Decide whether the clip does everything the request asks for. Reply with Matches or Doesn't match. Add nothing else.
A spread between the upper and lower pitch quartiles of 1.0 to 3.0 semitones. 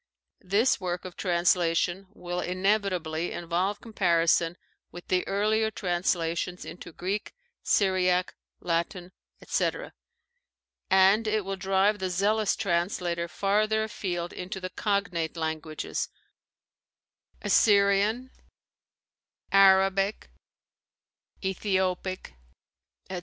Matches